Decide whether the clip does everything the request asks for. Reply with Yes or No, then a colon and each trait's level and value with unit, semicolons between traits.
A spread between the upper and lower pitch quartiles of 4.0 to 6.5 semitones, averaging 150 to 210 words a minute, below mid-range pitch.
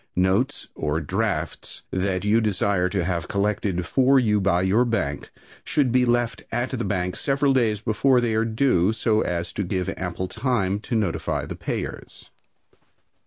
Yes: average, 4.5 semitones; average, 165 wpm; low, 105 Hz